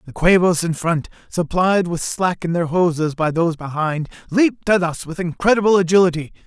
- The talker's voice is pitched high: No, medium, 170 Hz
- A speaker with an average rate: Yes, average, 175 wpm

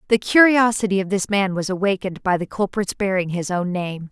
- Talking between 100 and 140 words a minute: No, fast, 205 wpm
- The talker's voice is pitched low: No, high, 195 Hz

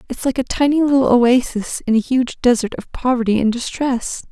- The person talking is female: Yes, female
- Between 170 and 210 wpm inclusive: Yes, average, 195 wpm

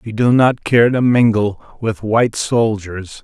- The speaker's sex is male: Yes, male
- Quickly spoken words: No, average, 165 wpm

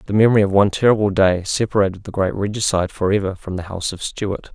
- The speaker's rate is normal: No, fast, 225 wpm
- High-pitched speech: No, low, 100 Hz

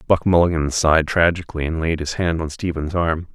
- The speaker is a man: Yes, male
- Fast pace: No, average, 195 wpm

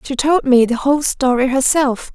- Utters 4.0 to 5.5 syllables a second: Yes, 4.9 syllables/s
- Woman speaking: Yes, female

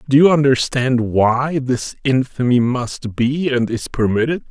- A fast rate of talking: No, average, 145 wpm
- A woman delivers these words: No, male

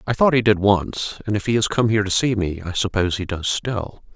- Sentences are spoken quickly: Yes, fast, 275 wpm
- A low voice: Yes, low, 105 Hz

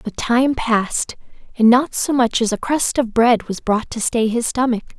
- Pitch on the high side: Yes, high, 235 Hz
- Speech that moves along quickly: Yes, fast, 215 wpm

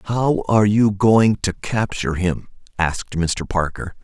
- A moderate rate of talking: Yes, average, 150 wpm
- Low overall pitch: Yes, low, 100 Hz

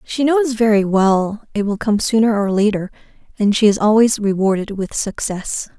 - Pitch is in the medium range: No, high, 210 Hz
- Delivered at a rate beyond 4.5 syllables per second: Yes, 4.7 syllables/s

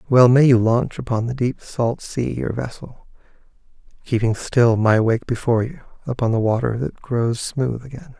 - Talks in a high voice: No, low, 120 Hz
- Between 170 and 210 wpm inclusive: Yes, average, 175 wpm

